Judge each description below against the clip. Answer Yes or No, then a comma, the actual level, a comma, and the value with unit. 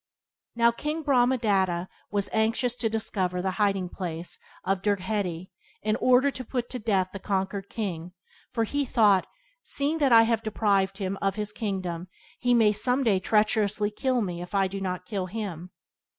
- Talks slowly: No, average, 165 wpm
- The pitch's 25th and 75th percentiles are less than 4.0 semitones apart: Yes, average, 3.5 semitones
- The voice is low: No, high, 205 Hz